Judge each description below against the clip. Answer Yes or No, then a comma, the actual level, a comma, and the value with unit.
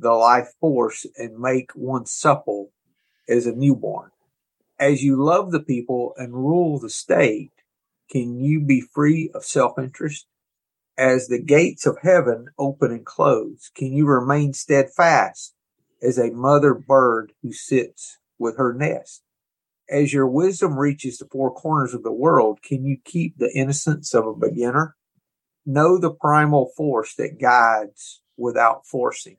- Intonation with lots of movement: No, average, 3.6 semitones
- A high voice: No, medium, 140 Hz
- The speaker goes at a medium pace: Yes, average, 150 wpm